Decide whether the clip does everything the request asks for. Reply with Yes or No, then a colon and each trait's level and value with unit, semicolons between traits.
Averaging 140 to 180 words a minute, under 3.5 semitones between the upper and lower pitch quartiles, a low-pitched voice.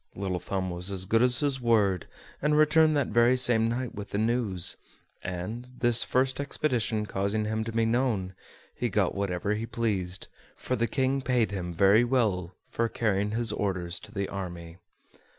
No: average, 175 wpm; average, 4.0 semitones; low, 110 Hz